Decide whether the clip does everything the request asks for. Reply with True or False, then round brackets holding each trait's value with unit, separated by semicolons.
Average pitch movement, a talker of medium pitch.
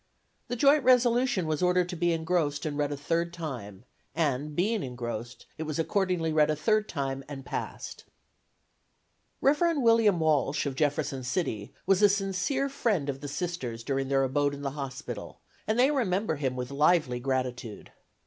False (6.0 semitones; 155 Hz)